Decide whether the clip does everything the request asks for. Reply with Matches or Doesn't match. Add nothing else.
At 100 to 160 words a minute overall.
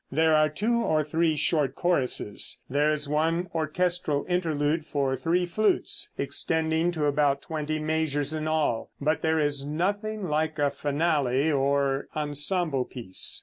Matches